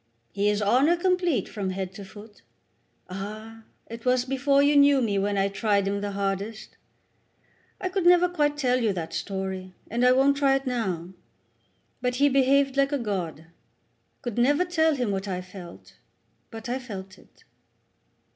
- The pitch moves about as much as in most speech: No, wide, 5.8 semitones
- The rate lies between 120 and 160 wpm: No, average, 175 wpm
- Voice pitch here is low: No, high, 230 Hz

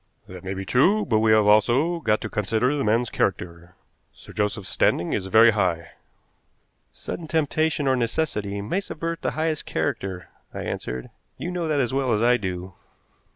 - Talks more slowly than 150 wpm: No, average, 175 wpm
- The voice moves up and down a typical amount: No, wide, 7.1 semitones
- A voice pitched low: Yes, low, 110 Hz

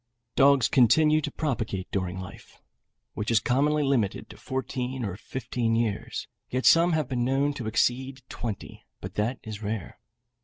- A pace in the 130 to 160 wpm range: Yes, average, 155 wpm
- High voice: No, low, 125 Hz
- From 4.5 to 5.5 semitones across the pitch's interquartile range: No, average, 4.0 semitones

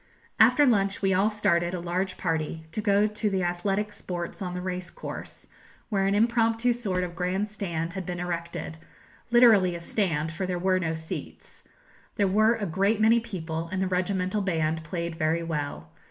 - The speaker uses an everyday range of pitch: Yes, average, 3.4 semitones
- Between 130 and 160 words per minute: No, average, 180 wpm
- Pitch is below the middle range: No, medium, 185 Hz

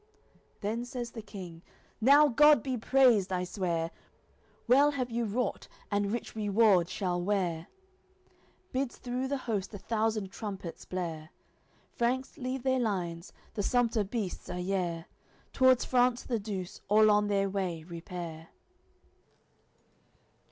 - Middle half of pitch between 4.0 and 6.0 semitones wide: Yes, average, 5.1 semitones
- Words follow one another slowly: Yes, slow, 130 wpm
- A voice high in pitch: Yes, high, 210 Hz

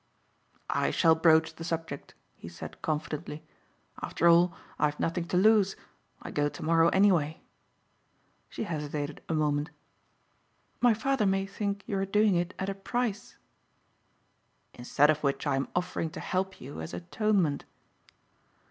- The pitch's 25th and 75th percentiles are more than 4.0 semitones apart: Yes, average, 4.6 semitones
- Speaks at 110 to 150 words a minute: Yes, average, 145 wpm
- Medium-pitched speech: Yes, medium, 165 Hz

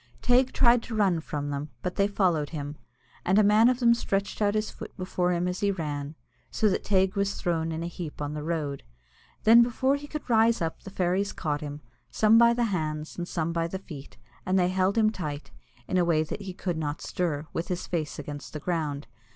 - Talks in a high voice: No, medium, 180 Hz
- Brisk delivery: Yes, fast, 225 wpm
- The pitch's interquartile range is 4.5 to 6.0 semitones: Yes, average, 5.0 semitones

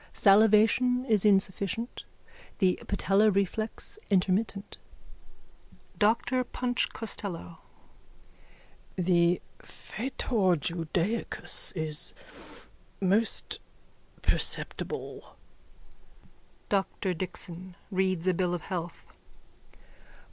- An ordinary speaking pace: No, slow, 70 wpm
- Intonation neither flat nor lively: Yes, average, 3.4 semitones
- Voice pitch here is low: No, high, 195 Hz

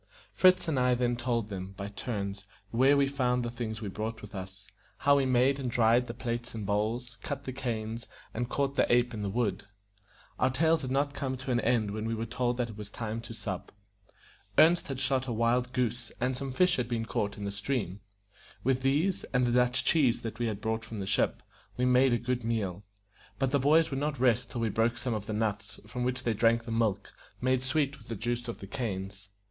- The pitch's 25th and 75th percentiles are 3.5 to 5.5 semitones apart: No, average, 2.9 semitones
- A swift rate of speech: Yes, fast, 230 wpm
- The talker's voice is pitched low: Yes, low, 120 Hz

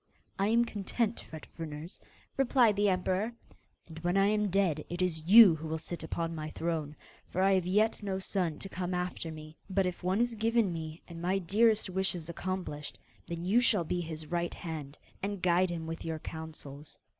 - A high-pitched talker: No, medium, 180 Hz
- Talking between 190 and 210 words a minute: Yes, average, 200 wpm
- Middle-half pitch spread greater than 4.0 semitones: No, average, 3.5 semitones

